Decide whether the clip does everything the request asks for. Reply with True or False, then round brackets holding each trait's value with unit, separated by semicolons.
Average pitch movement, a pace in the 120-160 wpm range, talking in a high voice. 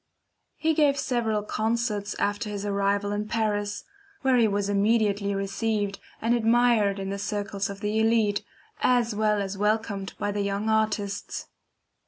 False (1.9 semitones; 150 wpm; 210 Hz)